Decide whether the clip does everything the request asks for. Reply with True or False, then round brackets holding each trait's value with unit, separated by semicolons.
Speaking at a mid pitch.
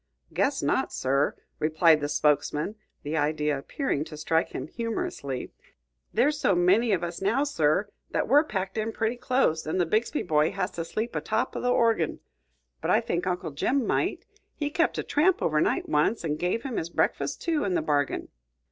True (180 Hz)